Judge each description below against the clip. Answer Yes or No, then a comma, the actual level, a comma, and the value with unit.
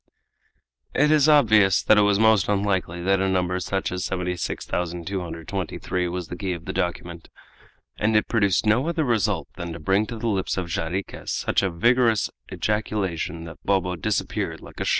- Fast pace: No, average, 175 wpm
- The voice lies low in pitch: Yes, very low, 95 Hz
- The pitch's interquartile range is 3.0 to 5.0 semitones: Yes, average, 3.5 semitones